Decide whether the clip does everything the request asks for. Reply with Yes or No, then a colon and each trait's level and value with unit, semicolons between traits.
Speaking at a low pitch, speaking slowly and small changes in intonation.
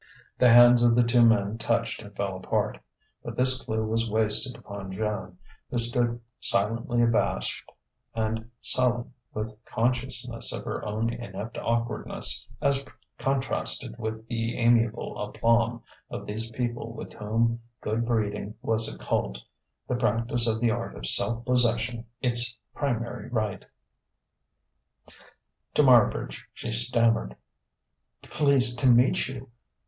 Yes: low, 115 Hz; slow, 130 wpm; narrow, 1.6 semitones